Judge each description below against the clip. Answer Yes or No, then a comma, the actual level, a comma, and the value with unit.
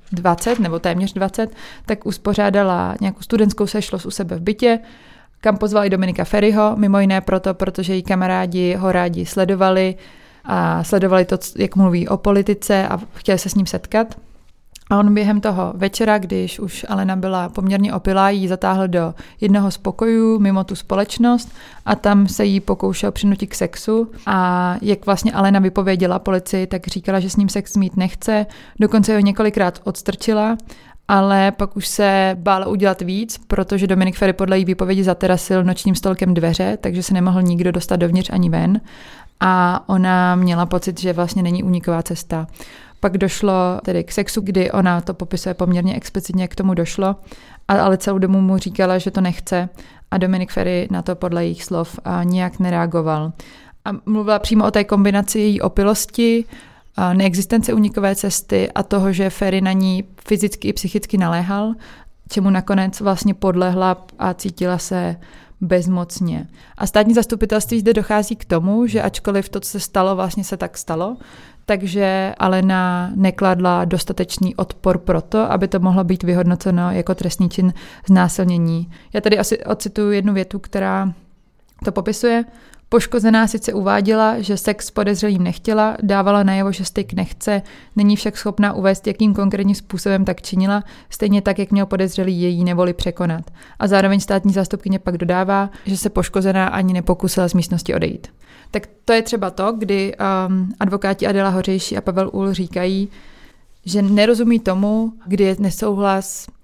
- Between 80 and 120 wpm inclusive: No, average, 160 wpm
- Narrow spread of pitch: Yes, narrow, 1.9 semitones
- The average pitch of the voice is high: Yes, high, 195 Hz